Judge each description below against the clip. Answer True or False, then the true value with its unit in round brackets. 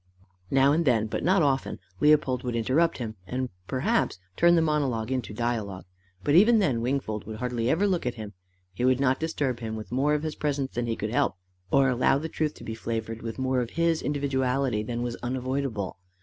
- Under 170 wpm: False (205 wpm)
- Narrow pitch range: False (4.0 semitones)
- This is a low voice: True (130 Hz)